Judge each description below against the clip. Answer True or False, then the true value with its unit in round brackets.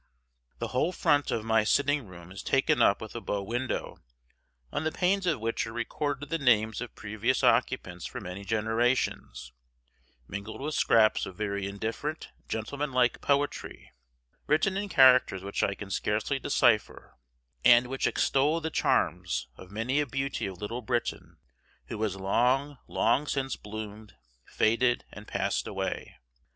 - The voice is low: True (120 Hz)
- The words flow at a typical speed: True (155 wpm)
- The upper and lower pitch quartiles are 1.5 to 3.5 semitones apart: False (4.8 semitones)